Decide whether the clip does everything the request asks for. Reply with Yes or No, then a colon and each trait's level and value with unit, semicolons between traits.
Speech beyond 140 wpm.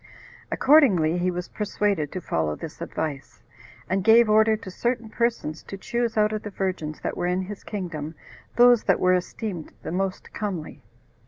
Yes: average, 170 wpm